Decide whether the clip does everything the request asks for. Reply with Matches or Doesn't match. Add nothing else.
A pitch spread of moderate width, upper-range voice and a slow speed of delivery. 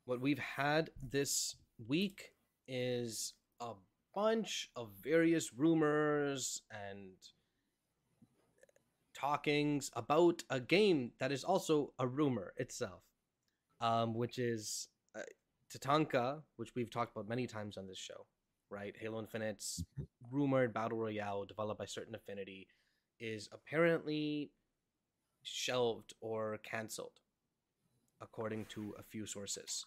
Doesn't match